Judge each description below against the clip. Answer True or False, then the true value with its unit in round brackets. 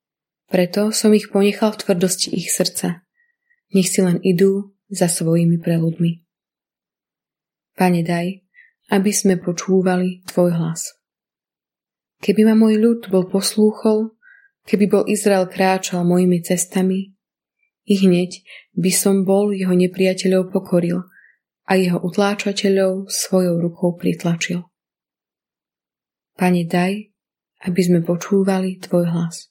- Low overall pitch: False (190 Hz)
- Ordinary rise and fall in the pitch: False (2.2 semitones)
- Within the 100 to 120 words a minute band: True (110 wpm)